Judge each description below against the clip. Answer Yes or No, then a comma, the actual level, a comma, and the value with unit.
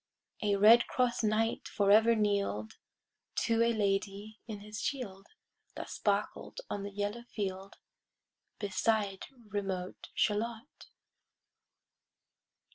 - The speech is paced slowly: Yes, slow, 110 wpm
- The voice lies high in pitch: Yes, high, 210 Hz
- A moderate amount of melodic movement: No, narrow, 2.2 semitones